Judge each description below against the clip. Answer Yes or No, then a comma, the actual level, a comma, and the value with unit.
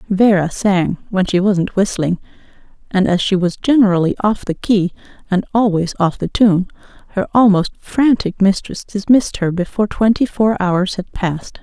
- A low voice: No, high, 195 Hz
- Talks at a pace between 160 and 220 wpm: No, average, 150 wpm